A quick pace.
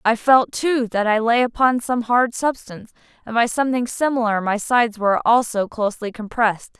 No: average, 175 wpm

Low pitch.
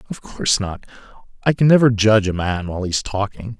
Yes: low, 105 Hz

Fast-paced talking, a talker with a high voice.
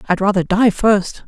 No: average, 190 wpm; high, 195 Hz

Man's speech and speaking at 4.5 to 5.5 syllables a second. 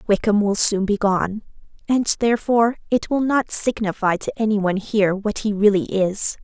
No: female; 5.1 syllables/s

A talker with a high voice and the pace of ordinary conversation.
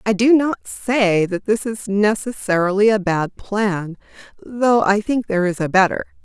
Yes: high, 205 Hz; average, 175 wpm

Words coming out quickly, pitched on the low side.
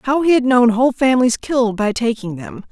No: fast, 220 wpm; high, 240 Hz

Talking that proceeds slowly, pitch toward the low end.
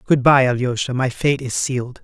No: fast, 205 wpm; low, 130 Hz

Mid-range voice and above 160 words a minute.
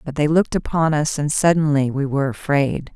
Yes: medium, 150 Hz; fast, 205 wpm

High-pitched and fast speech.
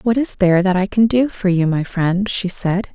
Yes: high, 195 Hz; fast, 265 wpm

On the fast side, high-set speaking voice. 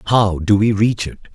No: fast, 225 wpm; low, 100 Hz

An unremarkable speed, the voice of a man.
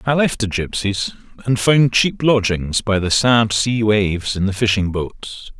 Yes: average, 180 wpm; male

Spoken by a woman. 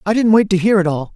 No: male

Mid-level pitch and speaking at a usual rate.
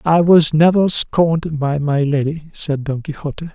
Yes: medium, 155 Hz; average, 170 wpm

